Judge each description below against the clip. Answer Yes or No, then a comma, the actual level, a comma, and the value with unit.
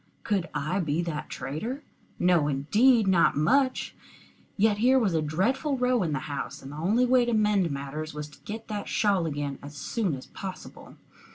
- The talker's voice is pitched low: No, medium, 185 Hz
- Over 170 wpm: Yes, average, 185 wpm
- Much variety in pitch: Yes, wide, 7.1 semitones